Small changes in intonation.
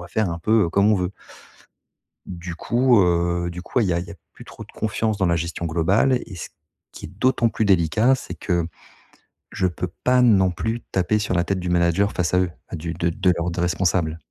No: average, 3.7 semitones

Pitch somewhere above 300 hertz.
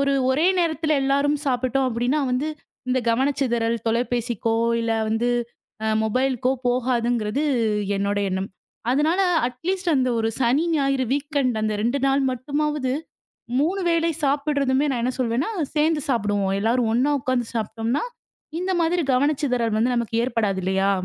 No: very high, 255 Hz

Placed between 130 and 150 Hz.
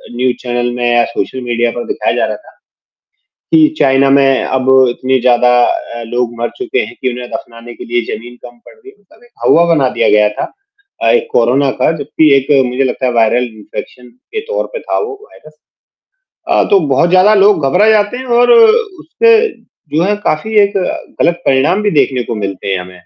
Yes: low, 135 Hz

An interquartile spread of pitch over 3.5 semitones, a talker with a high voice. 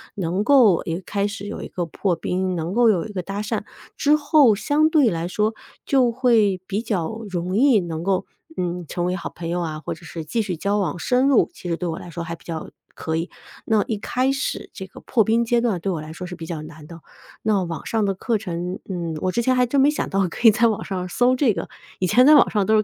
Yes: average, 5.1 semitones; high, 195 Hz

